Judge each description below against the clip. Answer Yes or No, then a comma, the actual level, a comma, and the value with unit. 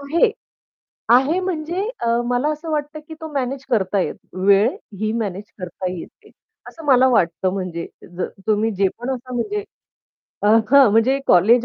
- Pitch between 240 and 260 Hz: Yes, high, 245 Hz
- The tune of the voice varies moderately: No, wide, 6.8 semitones